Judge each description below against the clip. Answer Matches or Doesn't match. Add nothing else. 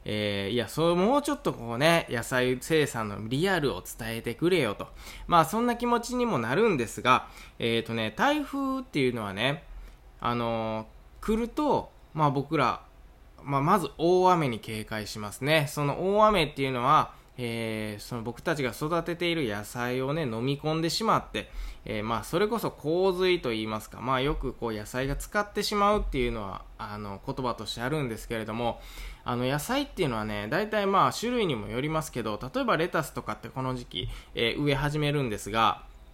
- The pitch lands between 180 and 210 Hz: Doesn't match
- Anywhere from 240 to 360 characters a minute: Matches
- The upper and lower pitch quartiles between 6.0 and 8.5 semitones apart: Matches